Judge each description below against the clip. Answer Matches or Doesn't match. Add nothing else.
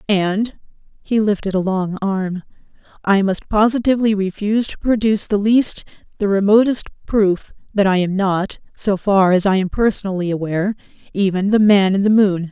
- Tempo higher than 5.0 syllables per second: Matches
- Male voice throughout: Doesn't match